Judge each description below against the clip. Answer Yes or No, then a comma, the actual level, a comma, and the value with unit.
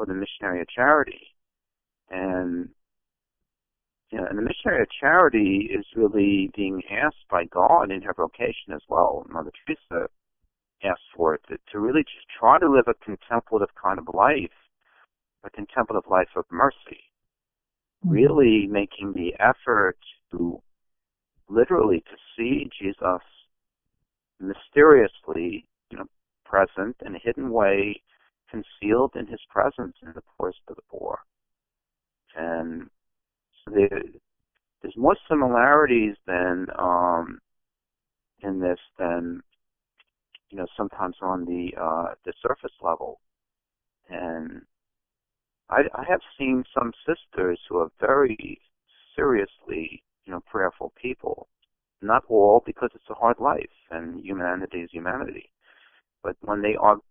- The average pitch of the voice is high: No, low, 100 Hz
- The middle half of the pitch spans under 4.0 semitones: Yes, average, 3.3 semitones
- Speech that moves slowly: Yes, slow, 125 wpm